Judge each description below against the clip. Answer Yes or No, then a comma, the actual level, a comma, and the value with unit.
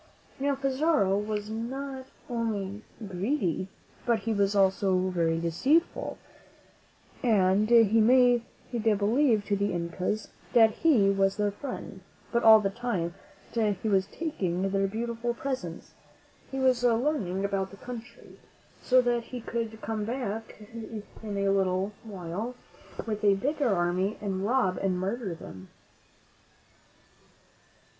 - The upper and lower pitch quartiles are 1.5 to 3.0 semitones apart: No, average, 3.7 semitones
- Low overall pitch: No, high, 215 Hz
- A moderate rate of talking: No, slow, 130 wpm